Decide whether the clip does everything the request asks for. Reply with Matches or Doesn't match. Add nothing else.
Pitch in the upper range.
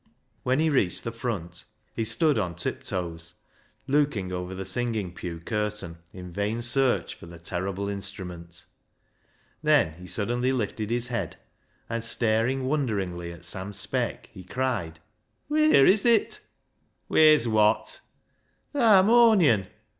Doesn't match